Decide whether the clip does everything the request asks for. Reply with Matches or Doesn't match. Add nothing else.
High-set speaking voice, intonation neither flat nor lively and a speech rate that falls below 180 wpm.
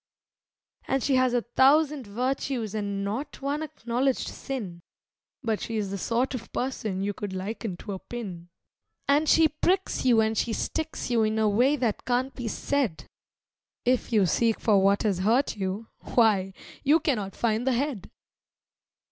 Matches